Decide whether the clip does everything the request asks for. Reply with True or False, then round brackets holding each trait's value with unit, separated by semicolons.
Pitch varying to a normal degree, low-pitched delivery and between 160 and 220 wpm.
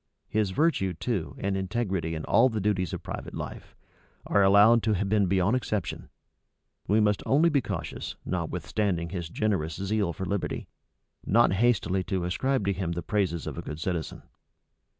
True (3.5 semitones; 95 Hz; 170 wpm)